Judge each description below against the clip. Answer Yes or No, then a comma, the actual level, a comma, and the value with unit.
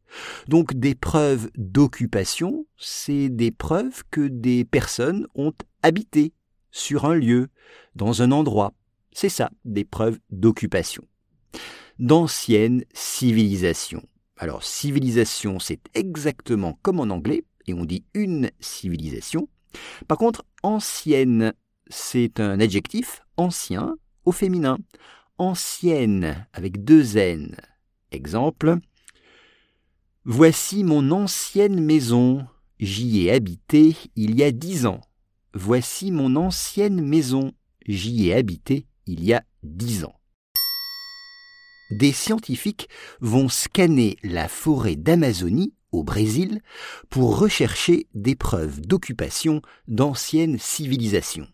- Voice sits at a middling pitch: No, low, 130 Hz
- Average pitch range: No, wide, 6.9 semitones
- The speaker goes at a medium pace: No, slow, 105 wpm